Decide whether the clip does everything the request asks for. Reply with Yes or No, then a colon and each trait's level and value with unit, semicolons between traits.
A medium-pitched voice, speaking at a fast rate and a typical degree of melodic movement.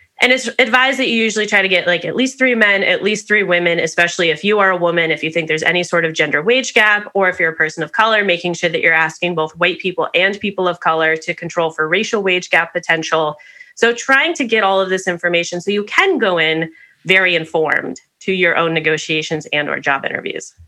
Yes: medium, 180 Hz; fast, 240 wpm; average, 4.1 semitones